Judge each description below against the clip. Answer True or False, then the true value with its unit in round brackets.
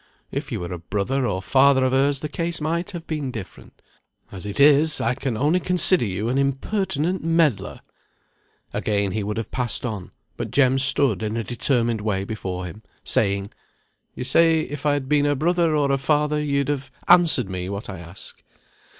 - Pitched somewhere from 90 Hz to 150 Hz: True (135 Hz)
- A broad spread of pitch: True (6.1 semitones)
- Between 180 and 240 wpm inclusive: True (190 wpm)